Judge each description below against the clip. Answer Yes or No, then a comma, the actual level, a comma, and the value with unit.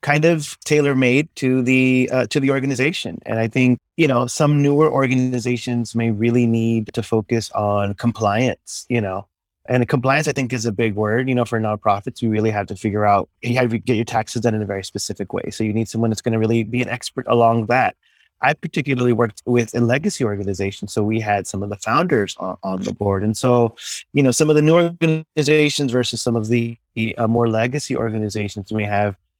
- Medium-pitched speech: No, low, 120 Hz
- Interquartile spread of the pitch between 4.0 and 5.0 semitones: No, average, 3.2 semitones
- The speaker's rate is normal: No, fast, 220 wpm